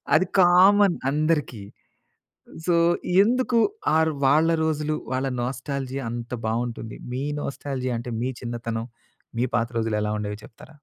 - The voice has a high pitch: No, low, 130 Hz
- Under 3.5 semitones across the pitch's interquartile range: No, average, 4.9 semitones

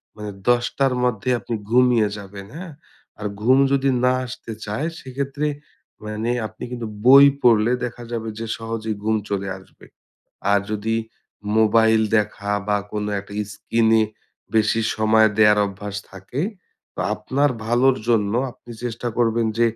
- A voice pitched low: Yes, low, 115 Hz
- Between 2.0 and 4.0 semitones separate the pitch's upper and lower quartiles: Yes, narrow, 2.5 semitones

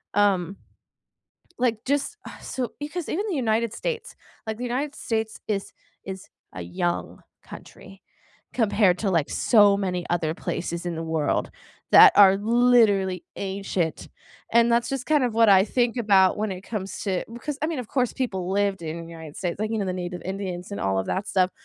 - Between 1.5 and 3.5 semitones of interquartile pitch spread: No, average, 4.6 semitones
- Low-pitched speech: No, high, 200 Hz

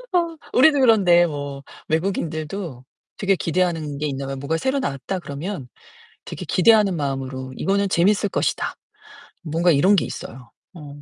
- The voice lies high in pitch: No, medium, 170 Hz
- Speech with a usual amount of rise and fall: No, wide, 5.8 semitones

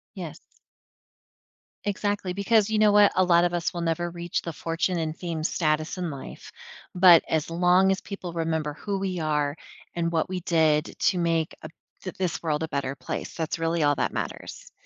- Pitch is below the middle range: No, medium, 170 Hz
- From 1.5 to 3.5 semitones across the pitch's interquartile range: Yes, narrow, 2.6 semitones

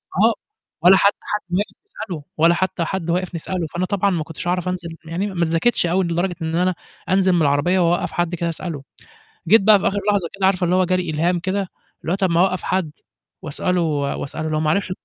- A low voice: No, medium, 180 Hz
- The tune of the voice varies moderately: No, narrow, 2.2 semitones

